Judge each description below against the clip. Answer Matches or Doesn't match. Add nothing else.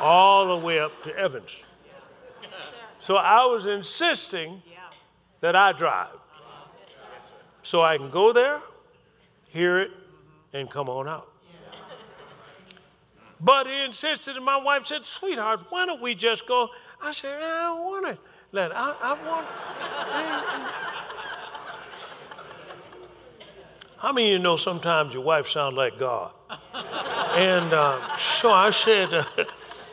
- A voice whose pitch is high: Matches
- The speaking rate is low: Matches